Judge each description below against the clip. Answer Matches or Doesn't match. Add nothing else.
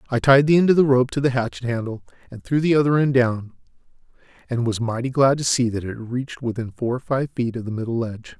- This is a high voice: Doesn't match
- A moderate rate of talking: Doesn't match